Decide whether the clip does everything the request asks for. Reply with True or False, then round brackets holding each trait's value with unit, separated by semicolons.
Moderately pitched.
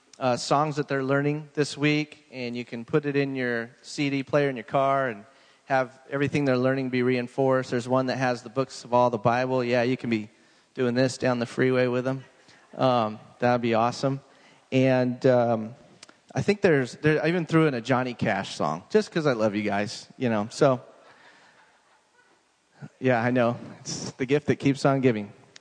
False (130 Hz)